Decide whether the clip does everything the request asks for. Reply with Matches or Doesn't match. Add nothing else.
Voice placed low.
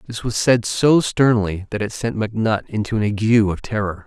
Matches